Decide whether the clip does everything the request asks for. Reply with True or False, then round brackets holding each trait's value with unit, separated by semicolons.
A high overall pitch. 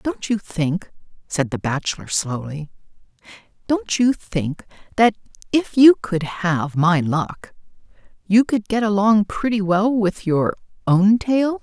True (195 Hz)